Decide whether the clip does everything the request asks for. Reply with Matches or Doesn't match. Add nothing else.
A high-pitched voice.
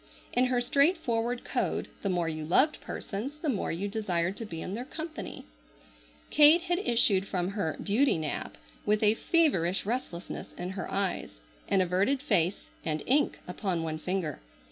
Matches